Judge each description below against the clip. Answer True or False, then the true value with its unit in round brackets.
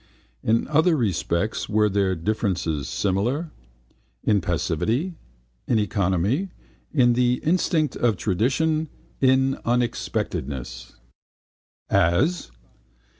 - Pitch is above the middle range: False (110 Hz)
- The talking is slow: True (85 wpm)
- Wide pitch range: True (6.6 semitones)